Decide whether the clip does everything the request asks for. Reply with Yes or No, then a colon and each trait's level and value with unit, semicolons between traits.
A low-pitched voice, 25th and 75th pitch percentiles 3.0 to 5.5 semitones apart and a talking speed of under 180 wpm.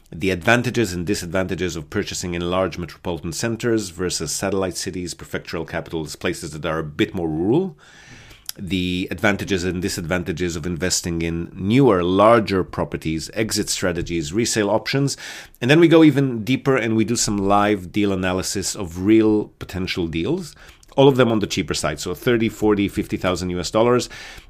Yes: very low, 95 Hz; average, 3.9 semitones; average, 160 wpm